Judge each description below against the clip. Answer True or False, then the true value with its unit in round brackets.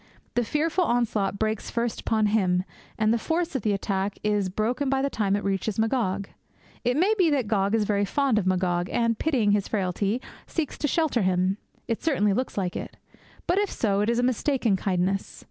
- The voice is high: True (215 Hz)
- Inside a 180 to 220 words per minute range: True (200 wpm)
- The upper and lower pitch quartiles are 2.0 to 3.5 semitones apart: False (4.4 semitones)